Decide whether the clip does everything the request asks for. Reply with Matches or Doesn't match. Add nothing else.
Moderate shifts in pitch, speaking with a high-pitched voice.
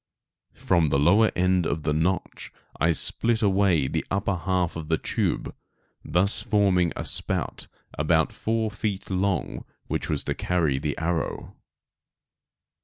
Doesn't match